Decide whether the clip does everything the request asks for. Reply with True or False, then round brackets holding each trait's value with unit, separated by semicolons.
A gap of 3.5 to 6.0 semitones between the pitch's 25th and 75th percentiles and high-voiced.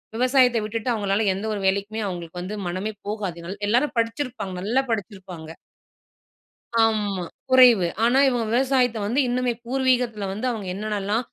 True (4.0 semitones; 220 Hz)